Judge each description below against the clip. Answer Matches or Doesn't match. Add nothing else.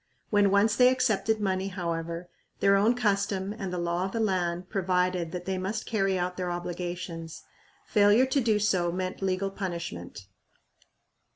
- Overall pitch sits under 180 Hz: Doesn't match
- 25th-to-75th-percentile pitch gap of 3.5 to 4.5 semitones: Doesn't match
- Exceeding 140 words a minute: Matches